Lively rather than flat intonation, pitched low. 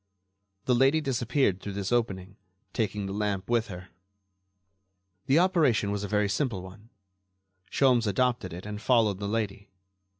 No: average, 3.8 semitones; low, 105 Hz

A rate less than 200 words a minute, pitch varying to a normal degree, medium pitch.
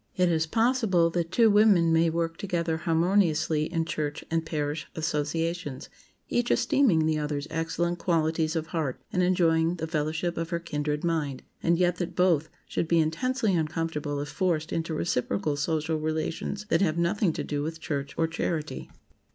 No: average, 165 wpm; narrow, 2.0 semitones; medium, 165 Hz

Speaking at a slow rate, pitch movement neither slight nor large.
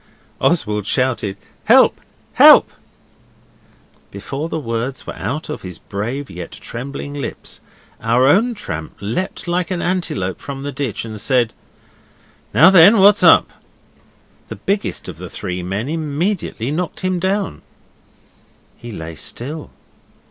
No: slow, 130 wpm; wide, 8.3 semitones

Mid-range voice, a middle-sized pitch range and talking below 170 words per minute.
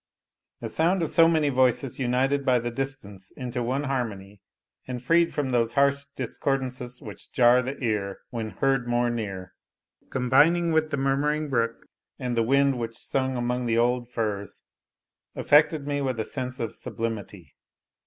No: low, 125 Hz; average, 3.0 semitones; average, 160 wpm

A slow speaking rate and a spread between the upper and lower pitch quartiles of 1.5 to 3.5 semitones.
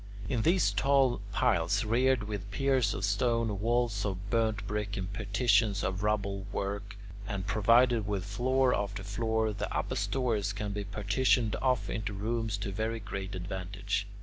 No: average, 155 wpm; average, 2.7 semitones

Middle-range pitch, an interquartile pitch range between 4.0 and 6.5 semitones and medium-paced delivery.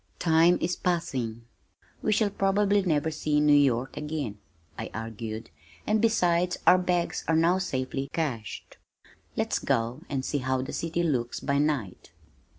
Yes: medium, 150 Hz; wide, 5.5 semitones; average, 155 wpm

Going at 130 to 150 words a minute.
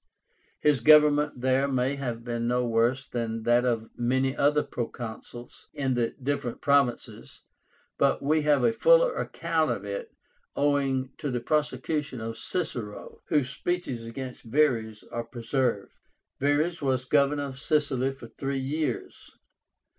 Yes: average, 140 wpm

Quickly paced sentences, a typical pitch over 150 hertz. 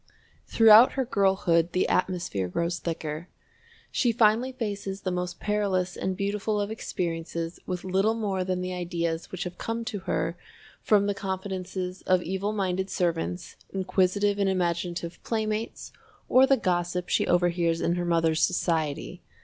No: average, 150 wpm; medium, 185 Hz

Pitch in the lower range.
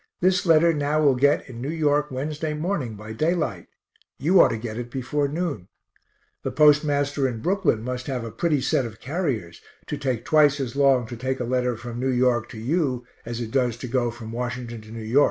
Yes: low, 130 Hz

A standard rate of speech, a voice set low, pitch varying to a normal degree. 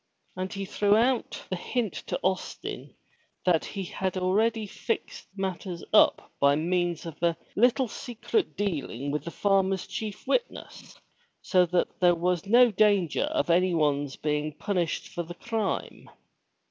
No: average, 145 wpm; medium, 185 Hz; average, 3.7 semitones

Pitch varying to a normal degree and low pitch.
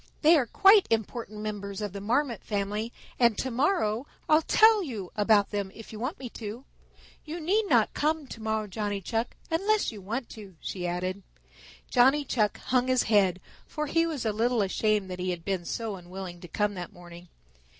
No: average, 5.0 semitones; high, 220 Hz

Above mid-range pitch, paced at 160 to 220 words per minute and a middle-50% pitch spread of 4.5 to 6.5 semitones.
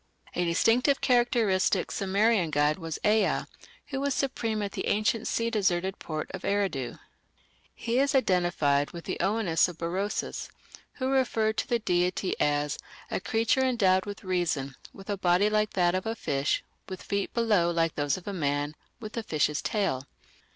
Yes: high, 195 Hz; average, 170 wpm; average, 4.9 semitones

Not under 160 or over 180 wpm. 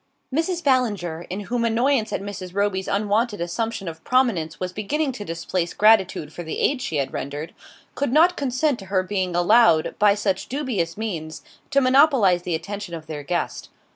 Yes: average, 175 wpm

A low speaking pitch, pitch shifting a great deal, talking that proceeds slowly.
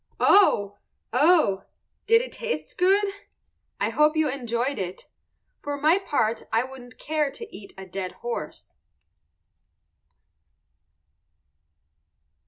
No: very high, 275 Hz; wide, 7.9 semitones; slow, 105 wpm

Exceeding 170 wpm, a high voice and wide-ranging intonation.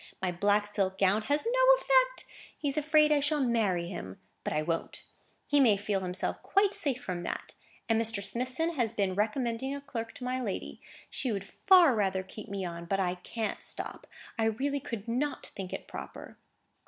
Yes: average, 190 wpm; high, 225 Hz; wide, 6.5 semitones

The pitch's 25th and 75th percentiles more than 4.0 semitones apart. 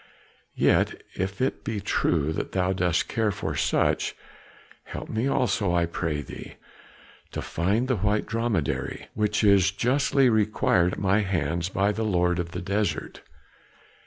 No: average, 3.5 semitones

